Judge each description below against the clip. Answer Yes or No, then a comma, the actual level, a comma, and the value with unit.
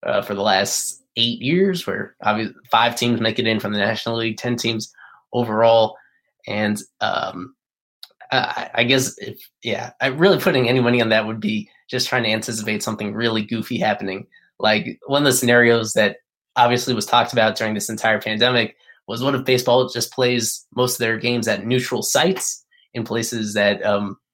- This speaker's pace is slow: No, average, 185 wpm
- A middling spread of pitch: No, narrow, 2.2 semitones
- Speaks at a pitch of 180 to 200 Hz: No, low, 120 Hz